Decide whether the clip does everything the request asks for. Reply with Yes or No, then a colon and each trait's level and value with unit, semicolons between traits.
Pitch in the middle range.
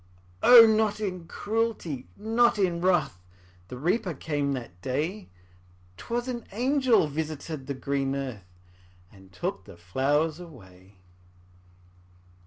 Yes: medium, 155 Hz